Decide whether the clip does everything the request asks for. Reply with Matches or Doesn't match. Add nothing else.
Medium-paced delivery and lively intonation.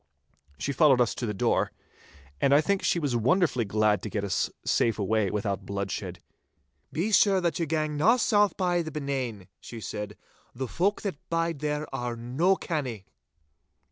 Matches